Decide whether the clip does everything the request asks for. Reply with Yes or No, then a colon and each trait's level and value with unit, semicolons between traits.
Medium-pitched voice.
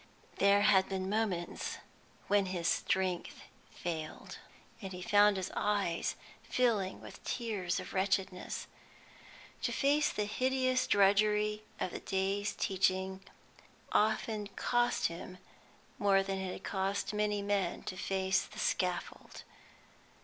No: high, 195 Hz